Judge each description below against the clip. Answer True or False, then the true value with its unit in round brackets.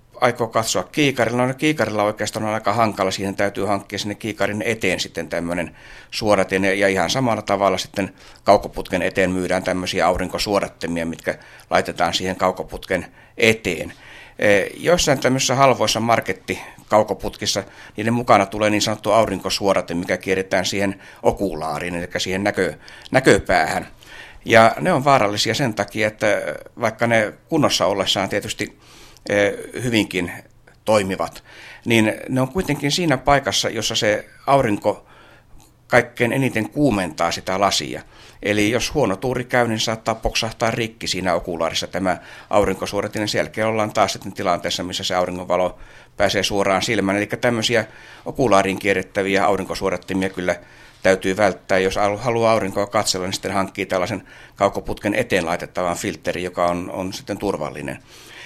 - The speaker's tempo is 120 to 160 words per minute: True (135 wpm)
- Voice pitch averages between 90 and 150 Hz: True (100 Hz)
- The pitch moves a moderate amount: True (3.1 semitones)